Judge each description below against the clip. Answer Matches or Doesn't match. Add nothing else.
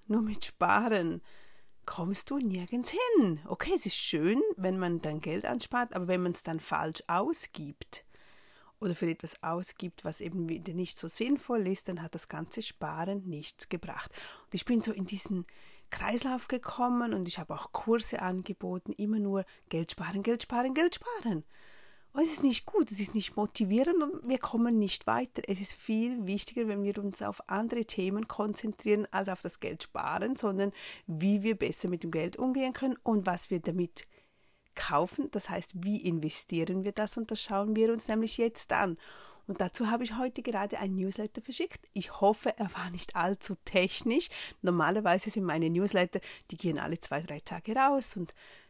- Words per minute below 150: Doesn't match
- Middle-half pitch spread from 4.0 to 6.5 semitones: Matches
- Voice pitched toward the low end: Doesn't match